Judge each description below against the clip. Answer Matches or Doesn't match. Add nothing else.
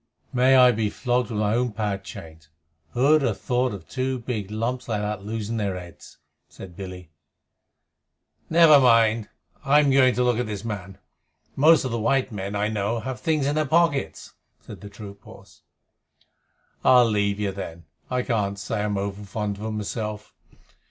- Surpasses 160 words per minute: Matches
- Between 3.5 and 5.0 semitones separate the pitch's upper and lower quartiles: Matches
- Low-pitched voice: Matches